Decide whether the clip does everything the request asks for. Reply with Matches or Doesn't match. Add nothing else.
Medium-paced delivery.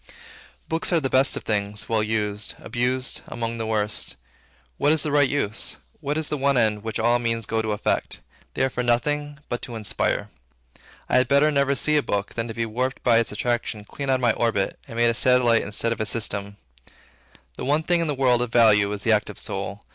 Doesn't match